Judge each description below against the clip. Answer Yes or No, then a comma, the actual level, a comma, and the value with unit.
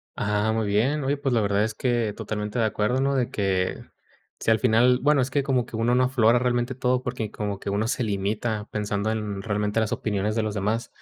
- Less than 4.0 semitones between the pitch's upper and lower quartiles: Yes, average, 3.1 semitones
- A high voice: No, low, 110 Hz